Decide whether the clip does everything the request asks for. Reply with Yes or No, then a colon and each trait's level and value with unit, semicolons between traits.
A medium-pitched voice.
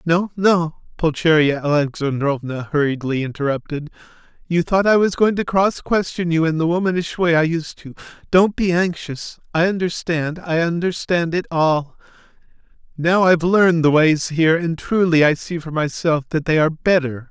Yes: medium, 165 Hz